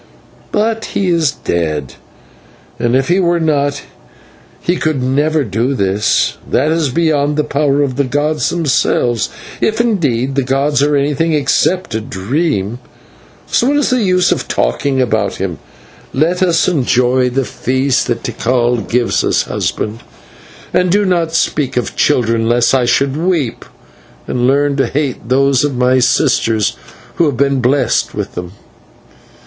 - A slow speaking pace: No, average, 155 wpm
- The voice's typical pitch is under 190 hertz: Yes, medium, 140 Hz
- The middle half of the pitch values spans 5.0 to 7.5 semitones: No, average, 4.2 semitones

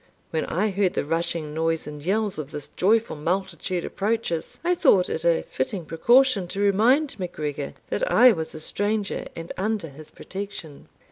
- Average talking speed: Yes, average, 175 wpm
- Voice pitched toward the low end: No, medium, 185 Hz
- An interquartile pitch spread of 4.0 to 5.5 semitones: Yes, average, 5.0 semitones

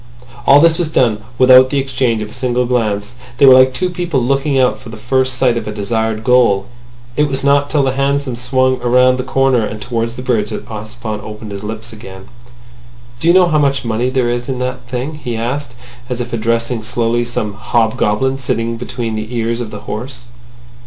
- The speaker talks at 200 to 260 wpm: Yes, fast, 205 wpm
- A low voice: Yes, low, 125 Hz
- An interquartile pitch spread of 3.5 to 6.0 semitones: No, average, 2.8 semitones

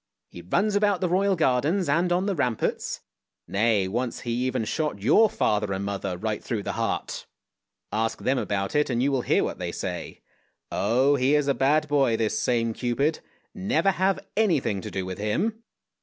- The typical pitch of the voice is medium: No, low, 130 Hz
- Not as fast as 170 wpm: No, average, 185 wpm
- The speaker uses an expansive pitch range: Yes, wide, 8.3 semitones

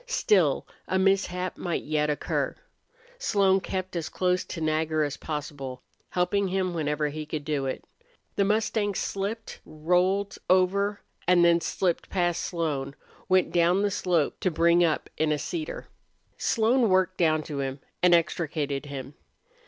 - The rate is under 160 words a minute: Yes, average, 150 wpm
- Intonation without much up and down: No, average, 3.8 semitones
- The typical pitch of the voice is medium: Yes, medium, 175 Hz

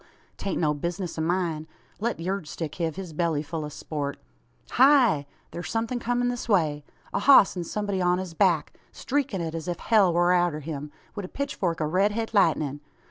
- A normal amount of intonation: Yes, average, 4.5 semitones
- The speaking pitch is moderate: Yes, medium, 175 Hz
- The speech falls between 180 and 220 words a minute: Yes, average, 190 wpm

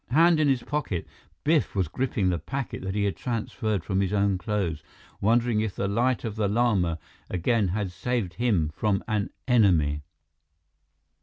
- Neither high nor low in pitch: No, low, 105 Hz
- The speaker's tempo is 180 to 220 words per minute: No, average, 165 wpm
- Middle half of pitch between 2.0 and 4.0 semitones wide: No, average, 4.6 semitones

